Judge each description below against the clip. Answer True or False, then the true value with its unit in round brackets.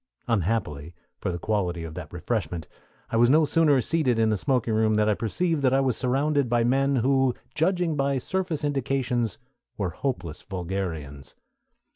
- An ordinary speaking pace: True (165 wpm)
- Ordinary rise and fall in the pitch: False (6.4 semitones)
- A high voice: False (120 Hz)